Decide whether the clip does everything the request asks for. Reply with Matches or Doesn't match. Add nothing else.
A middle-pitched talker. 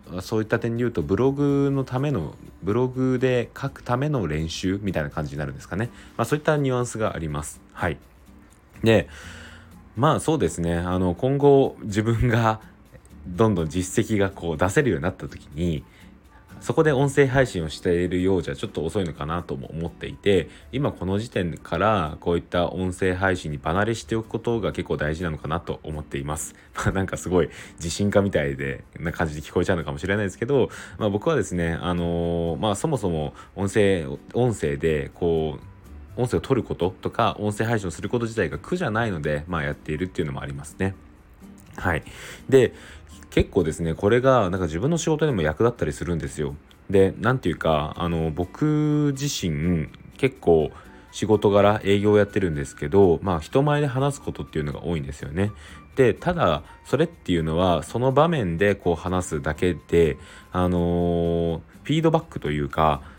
Doesn't match